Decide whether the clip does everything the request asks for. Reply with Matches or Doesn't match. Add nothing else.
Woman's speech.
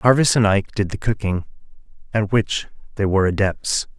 Doesn't match